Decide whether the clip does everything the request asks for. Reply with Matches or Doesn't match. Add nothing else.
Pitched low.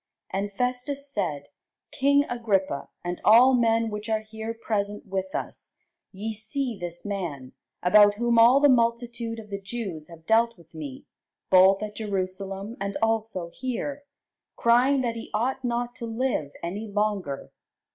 Doesn't match